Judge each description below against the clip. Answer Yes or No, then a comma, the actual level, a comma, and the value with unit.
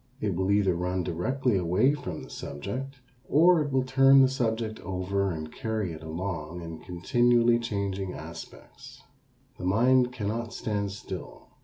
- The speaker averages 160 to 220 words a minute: No, average, 150 wpm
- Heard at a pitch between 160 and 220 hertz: No, low, 100 Hz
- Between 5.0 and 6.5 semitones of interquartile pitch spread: Yes, wide, 5.5 semitones